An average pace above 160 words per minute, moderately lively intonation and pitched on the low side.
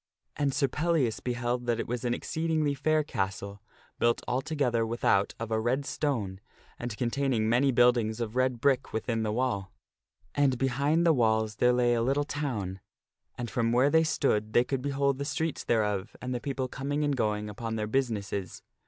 Yes: average, 180 wpm; average, 3.9 semitones; low, 125 Hz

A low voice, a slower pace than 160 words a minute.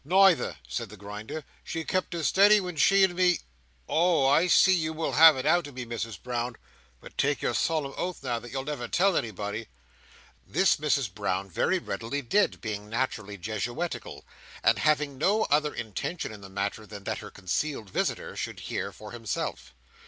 No: low, 130 Hz; average, 180 wpm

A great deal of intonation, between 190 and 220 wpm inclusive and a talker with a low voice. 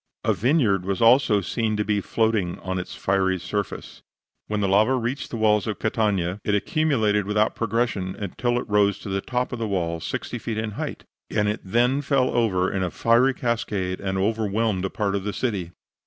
No: average, 3.1 semitones; average, 200 wpm; low, 105 Hz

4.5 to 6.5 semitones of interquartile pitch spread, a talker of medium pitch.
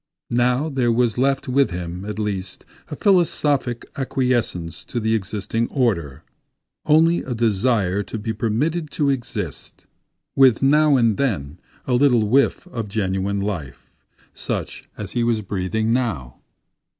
No: average, 4.9 semitones; low, 115 Hz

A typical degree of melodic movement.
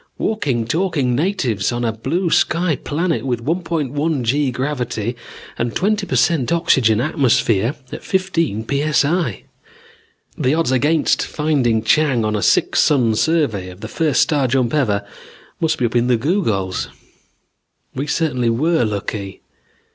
No: wide, 5.8 semitones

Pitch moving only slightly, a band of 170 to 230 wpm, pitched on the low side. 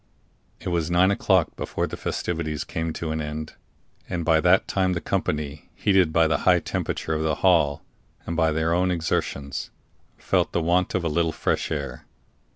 Yes: narrow, 2.1 semitones; average, 180 wpm; very low, 80 Hz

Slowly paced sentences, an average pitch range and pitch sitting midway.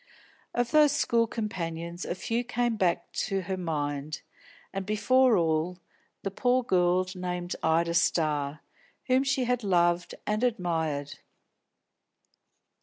No: slow, 120 wpm; wide, 5.7 semitones; medium, 180 Hz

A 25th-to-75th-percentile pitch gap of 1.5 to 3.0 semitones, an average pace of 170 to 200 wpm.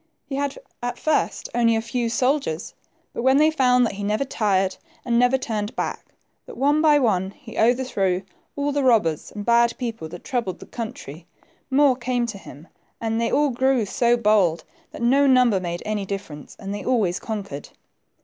No: average, 4.6 semitones; average, 185 wpm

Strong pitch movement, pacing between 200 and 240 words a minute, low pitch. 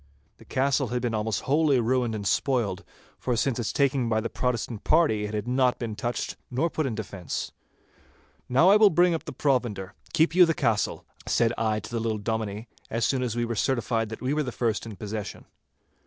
No: average, 3.5 semitones; fast, 205 wpm; low, 120 Hz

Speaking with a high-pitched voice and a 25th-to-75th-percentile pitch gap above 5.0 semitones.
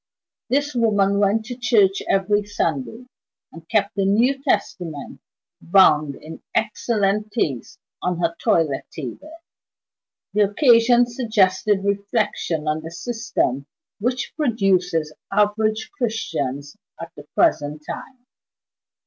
Yes: high, 200 Hz; wide, 5.5 semitones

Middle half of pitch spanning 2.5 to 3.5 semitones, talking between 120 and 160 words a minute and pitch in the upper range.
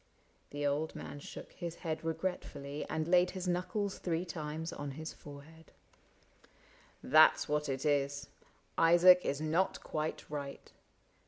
No: average, 3.1 semitones; average, 150 wpm; medium, 155 Hz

